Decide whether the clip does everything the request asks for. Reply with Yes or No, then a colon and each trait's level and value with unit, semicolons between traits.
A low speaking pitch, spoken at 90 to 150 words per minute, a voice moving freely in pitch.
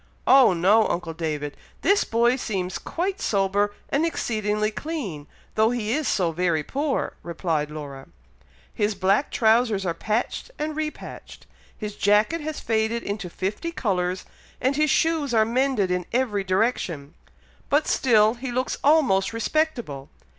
No: high, 215 Hz; average, 140 wpm; wide, 6.3 semitones